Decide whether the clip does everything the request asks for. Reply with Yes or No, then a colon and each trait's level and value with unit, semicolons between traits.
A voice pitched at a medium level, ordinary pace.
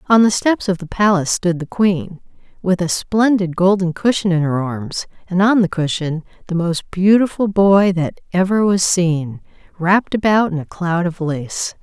Yes: medium, 180 Hz; average, 185 wpm